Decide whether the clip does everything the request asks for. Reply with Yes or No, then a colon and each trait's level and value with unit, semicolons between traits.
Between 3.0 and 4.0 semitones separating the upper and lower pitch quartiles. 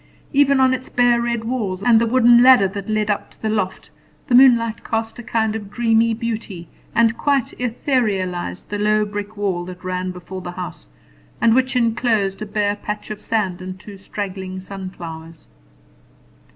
Yes: average, 3.7 semitones